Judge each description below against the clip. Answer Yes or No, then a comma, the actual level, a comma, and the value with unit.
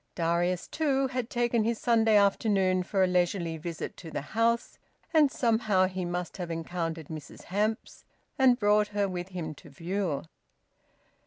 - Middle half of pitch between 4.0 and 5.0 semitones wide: Yes, average, 4.5 semitones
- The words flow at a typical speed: Yes, average, 155 wpm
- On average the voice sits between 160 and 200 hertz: Yes, high, 190 Hz